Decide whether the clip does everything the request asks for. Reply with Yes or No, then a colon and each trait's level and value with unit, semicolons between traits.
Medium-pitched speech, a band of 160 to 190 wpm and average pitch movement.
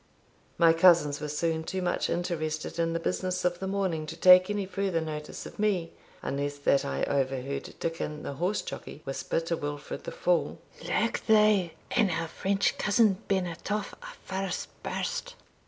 Yes: medium, 170 Hz; average, 170 wpm; average, 3.8 semitones